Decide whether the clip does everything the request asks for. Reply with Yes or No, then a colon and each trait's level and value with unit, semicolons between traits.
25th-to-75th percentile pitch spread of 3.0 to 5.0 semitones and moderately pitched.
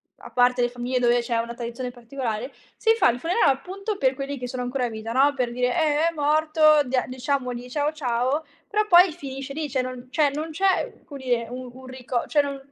No: average, 3.5 semitones; very high, 260 Hz